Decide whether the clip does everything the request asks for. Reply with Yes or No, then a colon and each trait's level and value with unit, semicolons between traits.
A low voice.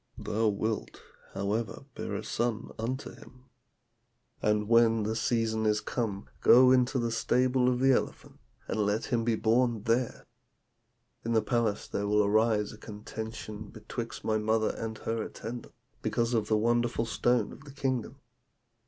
Yes: low, 115 Hz